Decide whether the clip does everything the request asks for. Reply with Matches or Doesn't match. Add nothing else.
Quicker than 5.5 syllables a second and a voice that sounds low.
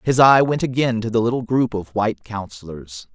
Doesn't match